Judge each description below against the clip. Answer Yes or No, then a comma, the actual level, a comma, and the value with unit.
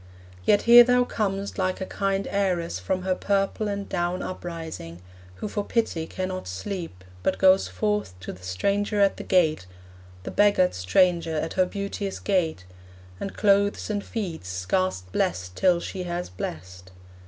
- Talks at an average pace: Yes, average, 155 wpm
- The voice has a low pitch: No, medium, 185 Hz